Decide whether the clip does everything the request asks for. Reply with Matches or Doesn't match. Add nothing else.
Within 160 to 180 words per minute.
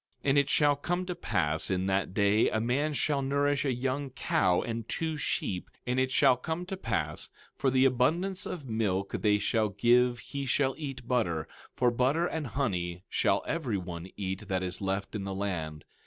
Doesn't match